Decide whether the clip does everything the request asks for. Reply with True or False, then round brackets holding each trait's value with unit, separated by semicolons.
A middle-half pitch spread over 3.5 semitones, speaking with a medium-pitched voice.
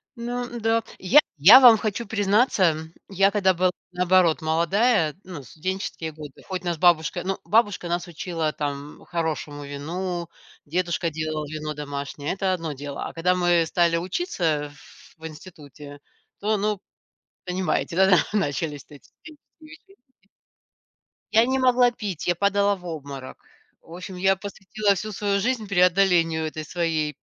True (4.3 semitones; 180 Hz)